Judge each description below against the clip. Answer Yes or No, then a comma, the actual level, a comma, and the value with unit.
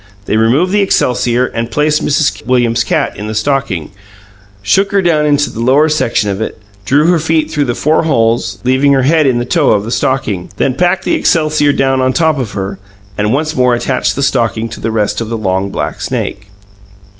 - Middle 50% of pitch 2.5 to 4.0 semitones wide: No, average, 5.0 semitones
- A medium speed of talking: No, fast, 210 wpm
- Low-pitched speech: Yes, low, 130 Hz